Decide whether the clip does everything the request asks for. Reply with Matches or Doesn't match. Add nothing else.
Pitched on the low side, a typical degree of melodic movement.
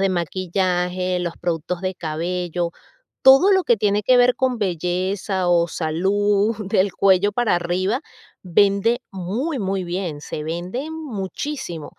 Doesn't match